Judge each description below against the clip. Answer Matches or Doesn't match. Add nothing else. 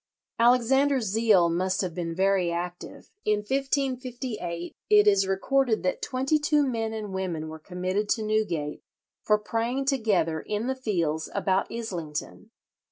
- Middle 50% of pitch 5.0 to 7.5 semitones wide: Matches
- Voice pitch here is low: Doesn't match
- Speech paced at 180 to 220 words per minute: Doesn't match